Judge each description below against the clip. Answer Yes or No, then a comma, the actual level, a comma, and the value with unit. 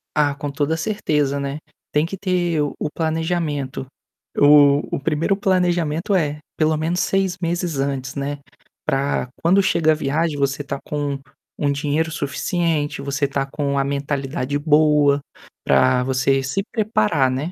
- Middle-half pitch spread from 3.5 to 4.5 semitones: No, average, 2.9 semitones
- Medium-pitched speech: Yes, medium, 145 Hz